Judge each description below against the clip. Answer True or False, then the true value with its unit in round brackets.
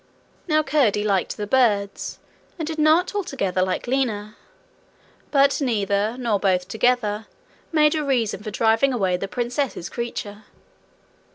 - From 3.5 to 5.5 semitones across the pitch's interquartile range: True (5.2 semitones)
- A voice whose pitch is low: False (230 Hz)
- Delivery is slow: True (130 wpm)